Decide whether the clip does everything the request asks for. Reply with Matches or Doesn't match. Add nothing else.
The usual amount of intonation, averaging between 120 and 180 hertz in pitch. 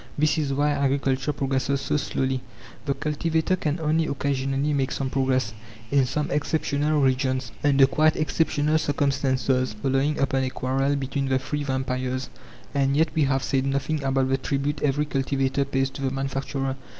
Doesn't match